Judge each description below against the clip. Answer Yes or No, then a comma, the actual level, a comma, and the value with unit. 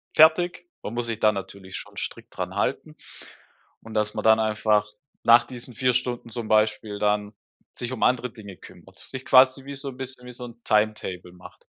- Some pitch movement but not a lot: Yes, average, 3.0 semitones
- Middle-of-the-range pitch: No, low, 115 Hz